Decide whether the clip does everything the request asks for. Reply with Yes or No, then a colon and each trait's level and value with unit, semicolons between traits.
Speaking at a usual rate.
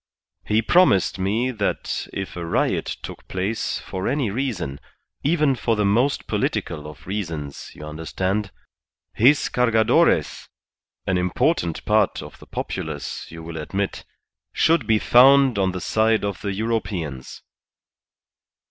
No: slow, 130 wpm